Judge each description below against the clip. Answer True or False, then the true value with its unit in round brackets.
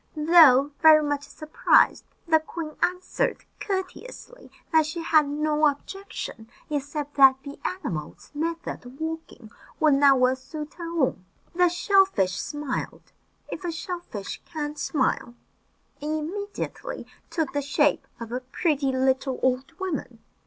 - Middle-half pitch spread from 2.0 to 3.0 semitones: False (3.8 semitones)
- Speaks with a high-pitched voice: True (300 Hz)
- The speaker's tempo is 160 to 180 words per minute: False (140 wpm)